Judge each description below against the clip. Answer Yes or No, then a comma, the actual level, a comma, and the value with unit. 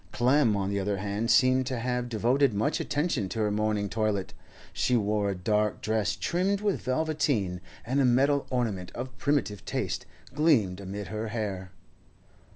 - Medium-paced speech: Yes, average, 160 wpm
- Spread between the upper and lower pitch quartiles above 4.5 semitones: No, average, 4.1 semitones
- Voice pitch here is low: Yes, low, 110 Hz